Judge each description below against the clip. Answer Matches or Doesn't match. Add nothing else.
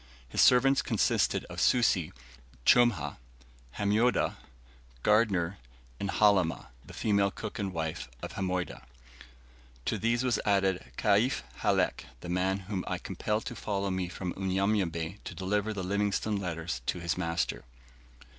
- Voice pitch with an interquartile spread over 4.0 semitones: Doesn't match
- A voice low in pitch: Matches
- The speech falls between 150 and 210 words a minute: Doesn't match